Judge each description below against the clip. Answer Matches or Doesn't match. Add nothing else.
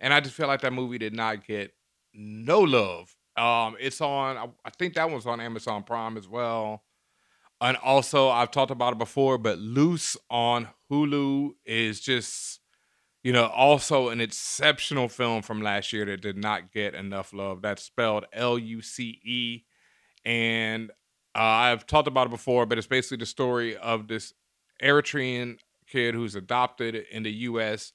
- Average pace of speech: Matches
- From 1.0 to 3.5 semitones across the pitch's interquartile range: Matches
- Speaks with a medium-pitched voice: Doesn't match